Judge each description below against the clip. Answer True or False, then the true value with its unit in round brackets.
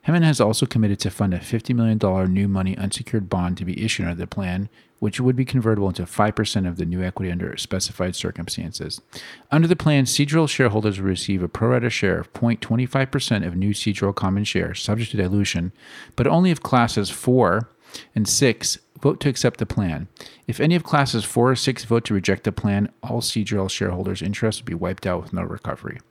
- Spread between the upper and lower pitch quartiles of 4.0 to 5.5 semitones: True (4.5 semitones)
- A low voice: True (105 Hz)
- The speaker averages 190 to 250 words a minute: True (200 wpm)